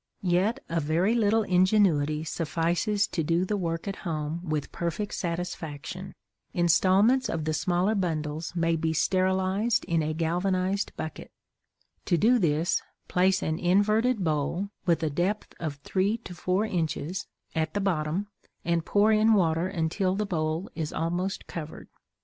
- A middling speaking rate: Yes, average, 150 wpm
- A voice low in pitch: No, medium, 175 Hz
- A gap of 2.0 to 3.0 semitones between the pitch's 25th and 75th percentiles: No, average, 3.6 semitones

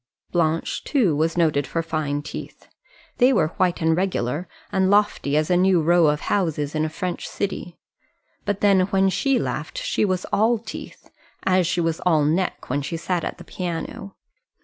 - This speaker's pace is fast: No, average, 180 wpm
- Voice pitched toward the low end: No, medium, 175 Hz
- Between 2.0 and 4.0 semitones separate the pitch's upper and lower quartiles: Yes, average, 3.5 semitones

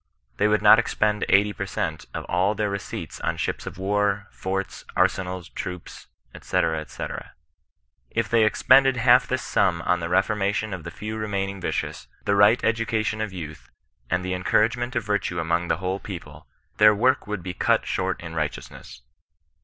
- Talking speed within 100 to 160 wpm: No, average, 170 wpm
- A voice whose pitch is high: No, low, 100 Hz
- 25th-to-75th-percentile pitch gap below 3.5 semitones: Yes, average, 2.9 semitones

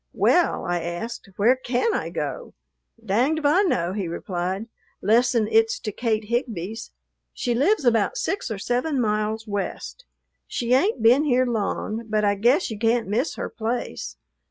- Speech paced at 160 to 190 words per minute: Yes, average, 165 wpm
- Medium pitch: No, high, 230 Hz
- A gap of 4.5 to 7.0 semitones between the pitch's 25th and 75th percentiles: No, average, 3.5 semitones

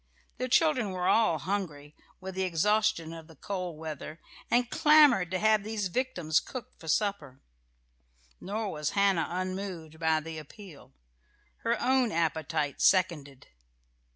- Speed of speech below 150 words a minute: Yes, slow, 135 wpm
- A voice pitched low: No, medium, 185 Hz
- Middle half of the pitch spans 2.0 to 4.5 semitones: No, average, 5.2 semitones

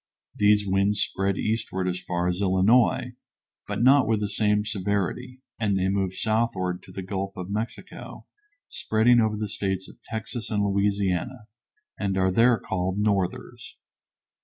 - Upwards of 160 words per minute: No, average, 150 wpm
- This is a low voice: Yes, low, 100 Hz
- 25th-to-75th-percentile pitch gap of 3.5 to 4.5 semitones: No, narrow, 2.5 semitones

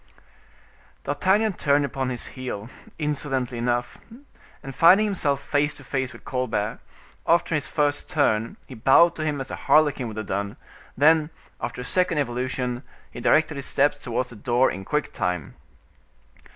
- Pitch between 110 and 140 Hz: Yes, low, 135 Hz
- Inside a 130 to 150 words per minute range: No, average, 160 wpm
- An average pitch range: Yes, average, 3.7 semitones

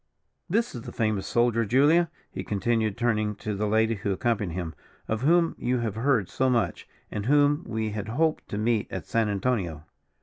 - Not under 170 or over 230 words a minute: Yes, average, 190 wpm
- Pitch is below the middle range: Yes, low, 110 Hz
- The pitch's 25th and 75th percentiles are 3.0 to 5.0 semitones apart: Yes, average, 3.5 semitones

